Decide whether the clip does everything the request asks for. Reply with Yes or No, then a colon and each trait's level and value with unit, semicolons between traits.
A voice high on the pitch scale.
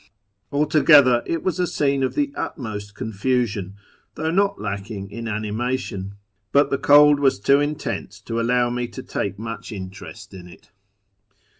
No: low, 120 Hz